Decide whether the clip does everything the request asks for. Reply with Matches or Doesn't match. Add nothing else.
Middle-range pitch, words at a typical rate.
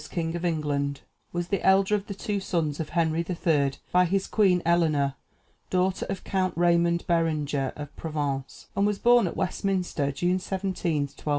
Matches